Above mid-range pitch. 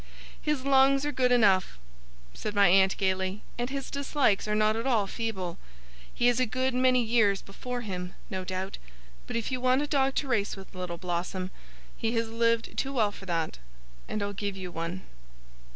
Yes: high, 215 Hz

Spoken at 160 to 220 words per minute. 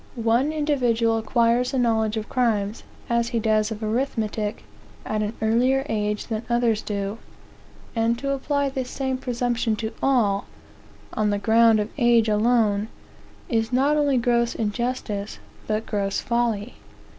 No: average, 145 wpm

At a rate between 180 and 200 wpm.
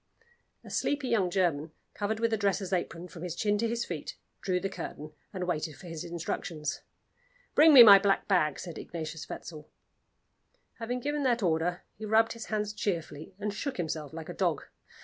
Yes: average, 185 wpm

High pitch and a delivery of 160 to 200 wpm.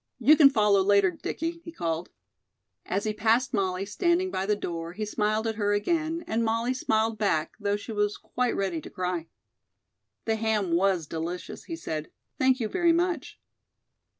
Yes: high, 210 Hz; average, 175 wpm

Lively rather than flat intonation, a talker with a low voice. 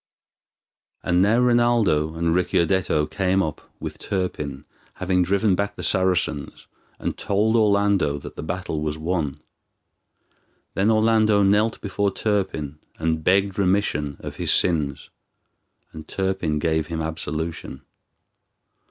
No: average, 4.4 semitones; very low, 90 Hz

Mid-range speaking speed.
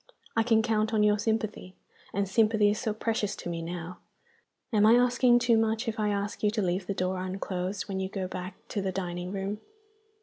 No: fast, 210 wpm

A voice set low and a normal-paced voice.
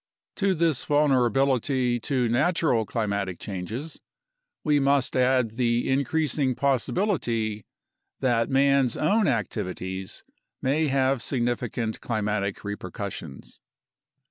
No: low, 125 Hz; slow, 100 wpm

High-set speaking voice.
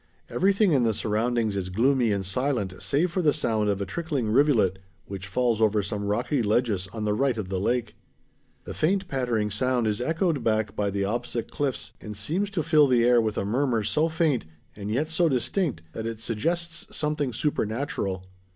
No: low, 120 Hz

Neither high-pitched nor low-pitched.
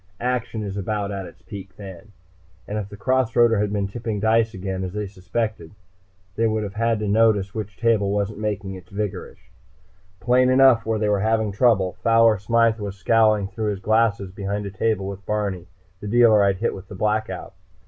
No: low, 105 Hz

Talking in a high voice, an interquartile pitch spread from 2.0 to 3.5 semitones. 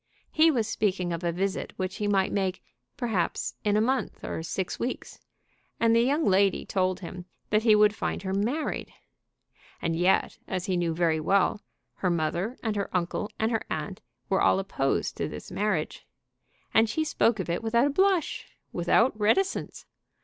No: high, 200 Hz; average, 3.9 semitones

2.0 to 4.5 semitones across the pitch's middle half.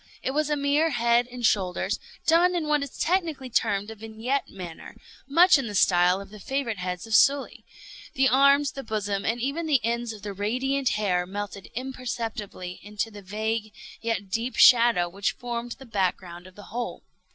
No: average, 5.0 semitones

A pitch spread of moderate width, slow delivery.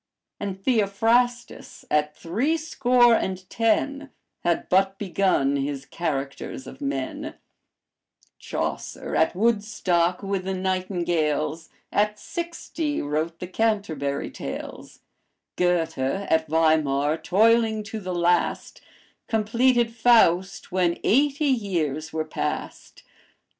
No: wide, 5.9 semitones; slow, 100 wpm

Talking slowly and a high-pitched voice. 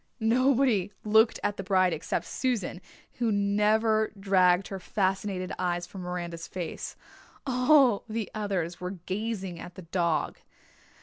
Yes: slow, 130 wpm; high, 195 Hz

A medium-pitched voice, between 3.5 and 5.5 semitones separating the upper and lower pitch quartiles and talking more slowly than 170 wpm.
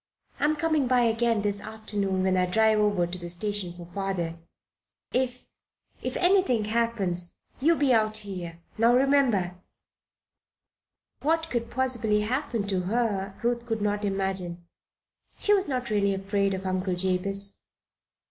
No: high, 210 Hz; average, 4.2 semitones; average, 140 wpm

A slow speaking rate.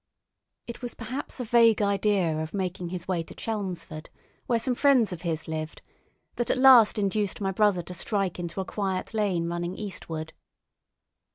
No: average, 170 wpm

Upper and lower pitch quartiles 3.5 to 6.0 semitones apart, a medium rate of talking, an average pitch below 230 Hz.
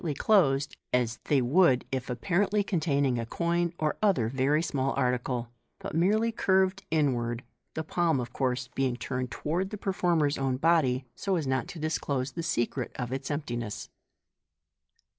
Yes: average, 5.2 semitones; average, 160 wpm; medium, 140 Hz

